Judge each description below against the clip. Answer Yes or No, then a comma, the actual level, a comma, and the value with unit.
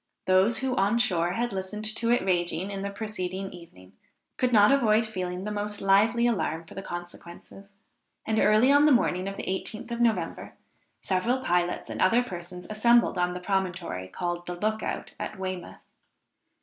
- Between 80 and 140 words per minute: No, average, 175 wpm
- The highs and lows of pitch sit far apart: No, average, 3.8 semitones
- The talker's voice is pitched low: No, high, 195 Hz